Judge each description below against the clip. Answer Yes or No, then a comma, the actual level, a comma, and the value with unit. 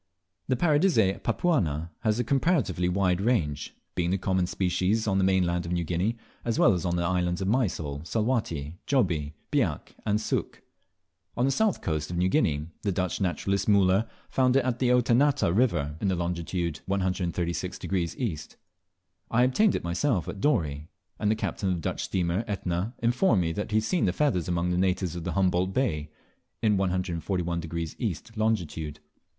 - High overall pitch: No, very low, 95 Hz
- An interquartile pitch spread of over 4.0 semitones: Yes, average, 4.7 semitones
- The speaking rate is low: No, average, 170 wpm